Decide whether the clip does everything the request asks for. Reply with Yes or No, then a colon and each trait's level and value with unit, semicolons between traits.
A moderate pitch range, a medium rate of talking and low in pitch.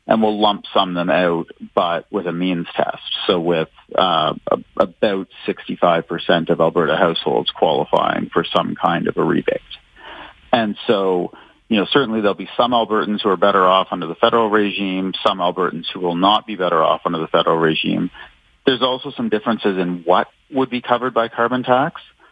Yes: average, 4.6 semitones; average, 185 wpm; low, 100 Hz